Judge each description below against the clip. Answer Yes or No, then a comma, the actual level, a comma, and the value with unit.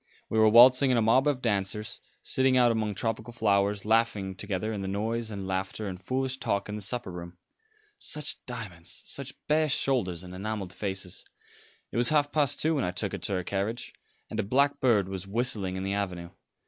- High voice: No, low, 110 Hz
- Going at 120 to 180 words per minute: No, average, 200 wpm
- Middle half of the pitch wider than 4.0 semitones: Yes, average, 4.4 semitones